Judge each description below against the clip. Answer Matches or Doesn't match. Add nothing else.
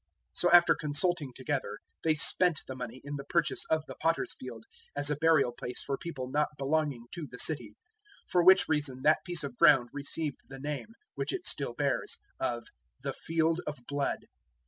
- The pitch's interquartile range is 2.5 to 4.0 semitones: Matches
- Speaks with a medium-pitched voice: Matches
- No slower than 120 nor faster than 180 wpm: Doesn't match